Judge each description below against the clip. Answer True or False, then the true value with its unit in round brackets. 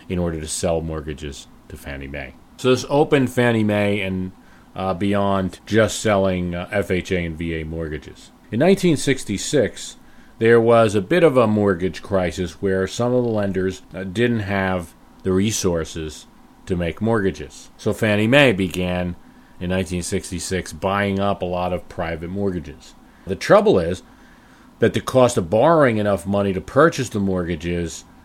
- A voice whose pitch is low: True (95 Hz)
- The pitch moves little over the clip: False (3.4 semitones)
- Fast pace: False (155 wpm)